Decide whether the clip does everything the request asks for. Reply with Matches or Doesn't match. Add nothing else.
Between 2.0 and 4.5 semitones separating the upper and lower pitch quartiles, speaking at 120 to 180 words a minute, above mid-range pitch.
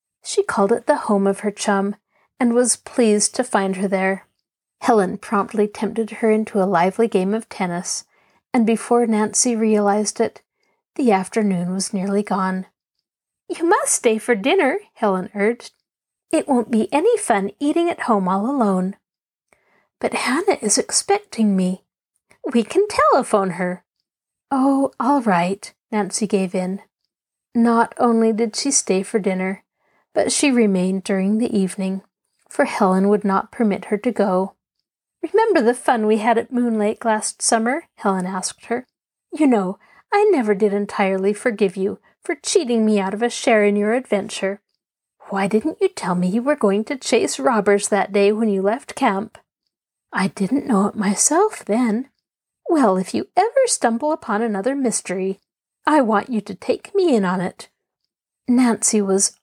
Matches